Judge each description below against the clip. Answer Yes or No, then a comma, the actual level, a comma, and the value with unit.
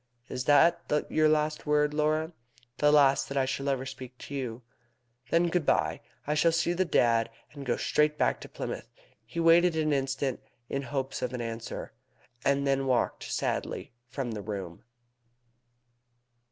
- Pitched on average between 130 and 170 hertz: Yes, medium, 140 Hz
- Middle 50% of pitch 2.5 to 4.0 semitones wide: Yes, average, 3.1 semitones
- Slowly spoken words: No, average, 165 wpm